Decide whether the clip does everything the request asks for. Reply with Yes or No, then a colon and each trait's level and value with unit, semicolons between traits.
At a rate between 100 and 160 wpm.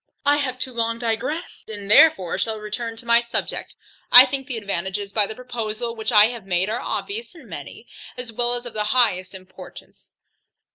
No: average, 190 wpm